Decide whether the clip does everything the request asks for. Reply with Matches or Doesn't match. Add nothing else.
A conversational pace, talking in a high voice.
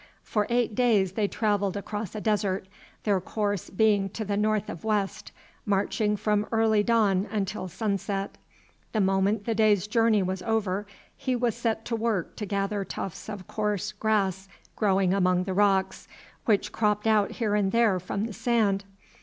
Matches